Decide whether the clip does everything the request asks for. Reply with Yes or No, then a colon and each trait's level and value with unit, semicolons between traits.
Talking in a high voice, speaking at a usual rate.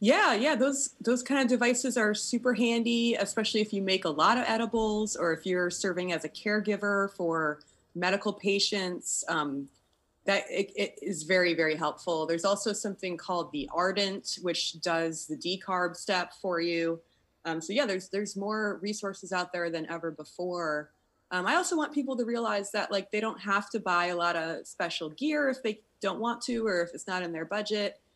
Yes: high, 195 Hz; average, 195 wpm